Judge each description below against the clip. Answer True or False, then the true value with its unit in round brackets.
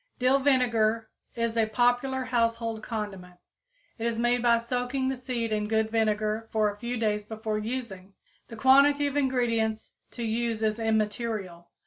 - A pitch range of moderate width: False (2.2 semitones)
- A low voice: False (230 Hz)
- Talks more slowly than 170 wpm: True (155 wpm)